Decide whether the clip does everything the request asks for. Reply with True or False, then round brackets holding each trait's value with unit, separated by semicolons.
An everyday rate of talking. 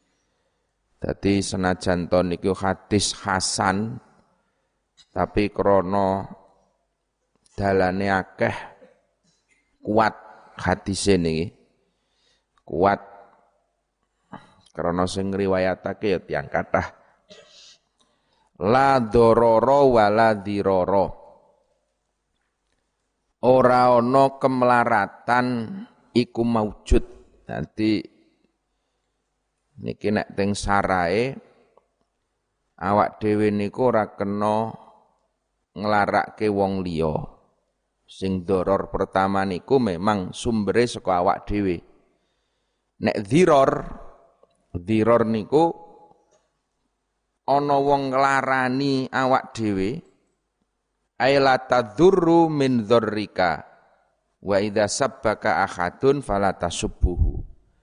False (70 wpm)